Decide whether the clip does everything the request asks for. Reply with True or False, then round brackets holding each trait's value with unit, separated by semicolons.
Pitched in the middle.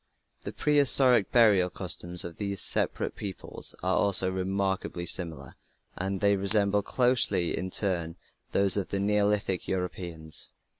False (95 Hz)